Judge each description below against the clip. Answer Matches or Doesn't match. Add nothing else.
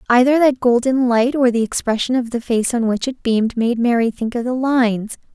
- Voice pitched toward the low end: Doesn't match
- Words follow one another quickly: Matches